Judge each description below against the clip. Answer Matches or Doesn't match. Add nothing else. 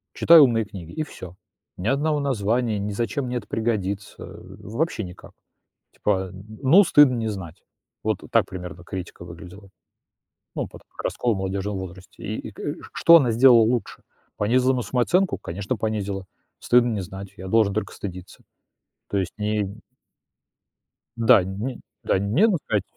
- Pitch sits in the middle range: Doesn't match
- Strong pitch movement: Doesn't match